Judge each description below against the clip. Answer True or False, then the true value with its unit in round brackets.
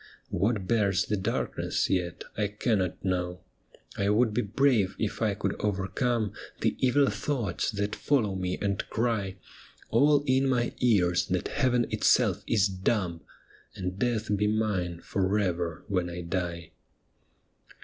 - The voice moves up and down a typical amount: True (4.0 semitones)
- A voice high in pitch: False (100 Hz)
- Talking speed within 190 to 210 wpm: False (140 wpm)